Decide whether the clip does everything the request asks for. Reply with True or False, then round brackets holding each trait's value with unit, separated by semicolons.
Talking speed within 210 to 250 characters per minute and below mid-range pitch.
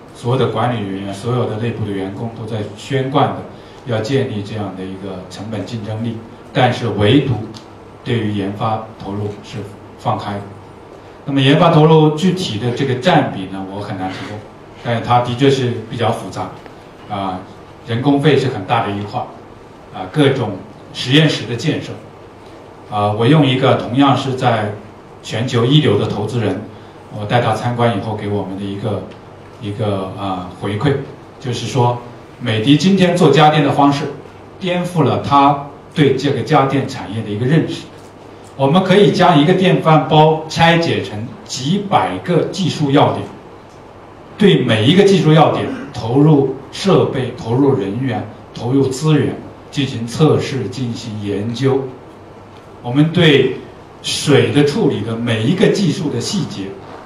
True (240 characters per minute; 120 Hz)